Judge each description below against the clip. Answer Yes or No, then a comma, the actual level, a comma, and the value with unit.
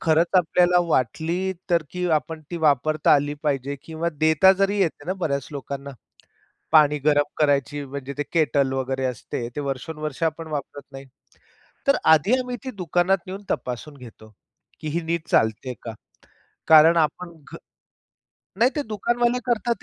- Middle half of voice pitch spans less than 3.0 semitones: No, average, 4.1 semitones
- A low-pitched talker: No, medium, 155 Hz